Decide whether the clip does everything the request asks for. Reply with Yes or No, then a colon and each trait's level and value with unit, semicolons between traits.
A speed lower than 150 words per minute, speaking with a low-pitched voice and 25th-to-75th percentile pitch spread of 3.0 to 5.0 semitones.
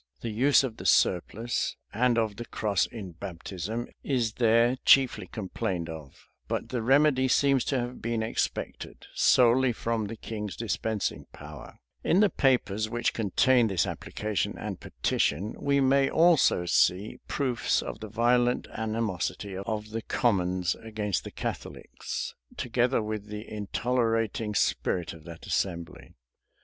Yes: average, 140 wpm; low, 110 Hz; average, 3.5 semitones